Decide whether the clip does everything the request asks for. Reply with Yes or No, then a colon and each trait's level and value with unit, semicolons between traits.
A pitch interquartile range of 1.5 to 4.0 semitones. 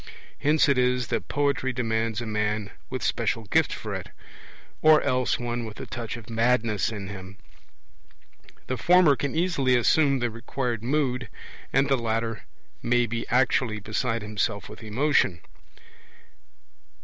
Yes: average, 3.0 semitones